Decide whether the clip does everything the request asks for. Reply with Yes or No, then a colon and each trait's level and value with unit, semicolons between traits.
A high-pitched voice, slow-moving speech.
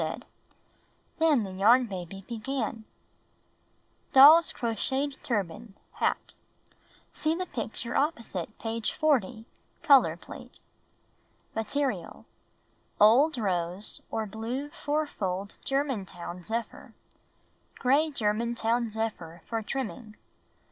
Yes: high, 230 Hz; slow, 95 wpm